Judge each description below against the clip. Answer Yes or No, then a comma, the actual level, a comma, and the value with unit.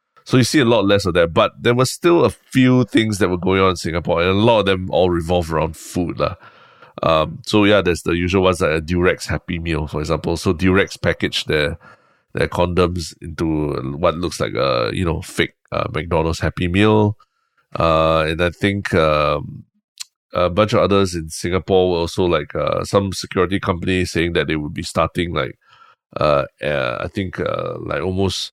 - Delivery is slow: No, average, 200 wpm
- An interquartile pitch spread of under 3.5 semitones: Yes, average, 3.1 semitones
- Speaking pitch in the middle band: No, very low, 90 Hz